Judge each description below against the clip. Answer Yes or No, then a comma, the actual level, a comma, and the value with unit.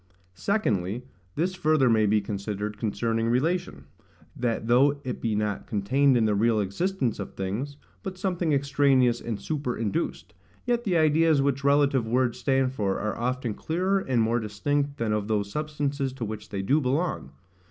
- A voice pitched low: Yes, low, 125 Hz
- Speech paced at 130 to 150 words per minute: No, average, 165 wpm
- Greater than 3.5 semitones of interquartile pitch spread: Yes, average, 5.2 semitones